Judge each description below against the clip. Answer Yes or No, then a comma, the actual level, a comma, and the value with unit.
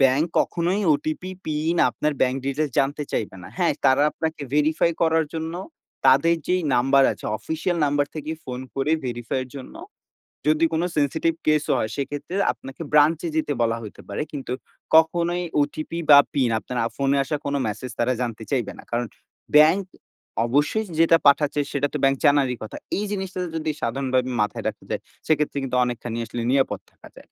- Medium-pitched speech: Yes, medium, 145 Hz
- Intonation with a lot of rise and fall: No, average, 3.7 semitones